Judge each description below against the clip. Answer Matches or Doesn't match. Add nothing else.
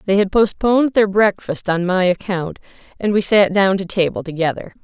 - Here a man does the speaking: Doesn't match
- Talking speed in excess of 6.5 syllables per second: Doesn't match